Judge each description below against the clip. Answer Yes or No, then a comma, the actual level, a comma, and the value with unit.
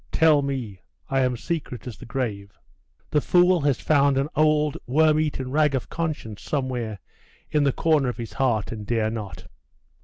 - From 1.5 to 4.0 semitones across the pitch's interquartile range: No, average, 4.6 semitones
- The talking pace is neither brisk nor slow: Yes, average, 175 wpm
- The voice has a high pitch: No, low, 135 Hz